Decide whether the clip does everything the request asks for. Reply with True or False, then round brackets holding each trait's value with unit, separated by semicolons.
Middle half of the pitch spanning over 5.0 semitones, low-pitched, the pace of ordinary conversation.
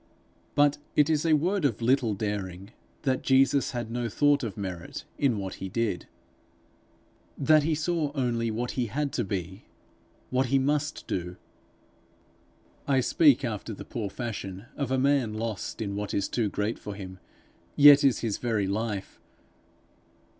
True (5.4 semitones; 120 Hz; 160 wpm)